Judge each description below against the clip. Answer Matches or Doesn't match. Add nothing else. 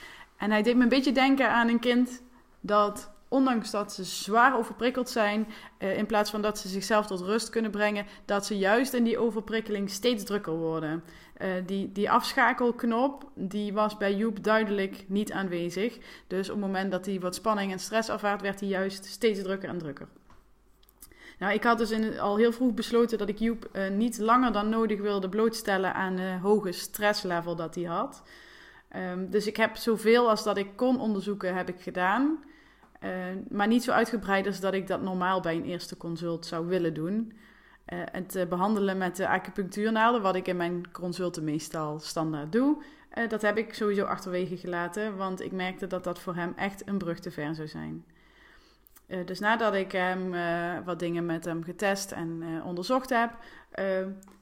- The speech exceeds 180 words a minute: Matches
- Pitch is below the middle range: Doesn't match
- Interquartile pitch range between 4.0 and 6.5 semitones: Doesn't match